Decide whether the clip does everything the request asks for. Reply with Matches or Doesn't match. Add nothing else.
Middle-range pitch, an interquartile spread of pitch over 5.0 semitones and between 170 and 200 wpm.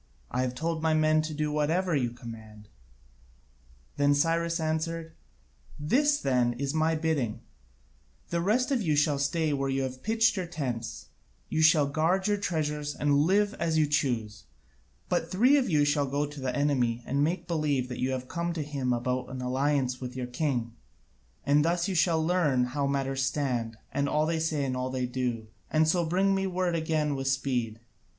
Doesn't match